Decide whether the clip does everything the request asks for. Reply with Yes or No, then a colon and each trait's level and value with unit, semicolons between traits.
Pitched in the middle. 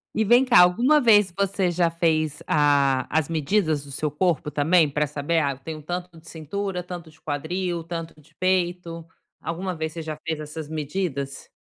Yes: medium, 165 Hz